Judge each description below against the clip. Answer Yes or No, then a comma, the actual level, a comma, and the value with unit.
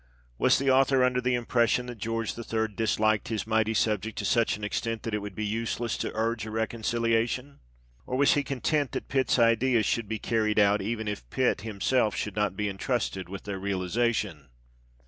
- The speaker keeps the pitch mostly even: Yes, narrow, 2.3 semitones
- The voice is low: Yes, low, 110 Hz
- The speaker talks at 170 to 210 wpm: Yes, average, 190 wpm